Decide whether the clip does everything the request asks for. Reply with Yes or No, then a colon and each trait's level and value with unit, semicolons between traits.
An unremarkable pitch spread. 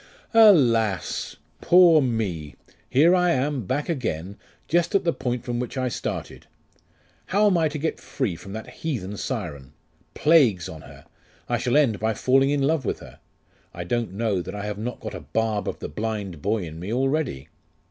No: wide, 6.6 semitones